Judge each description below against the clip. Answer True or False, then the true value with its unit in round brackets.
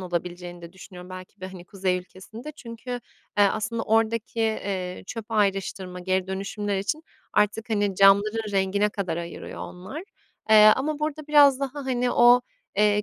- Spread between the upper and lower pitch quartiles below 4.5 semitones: True (3.6 semitones)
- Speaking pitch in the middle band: False (205 Hz)